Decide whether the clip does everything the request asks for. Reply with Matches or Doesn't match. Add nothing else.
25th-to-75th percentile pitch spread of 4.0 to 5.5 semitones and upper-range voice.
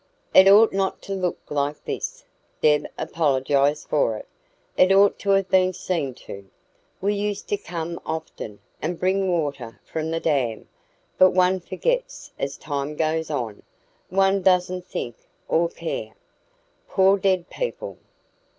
Doesn't match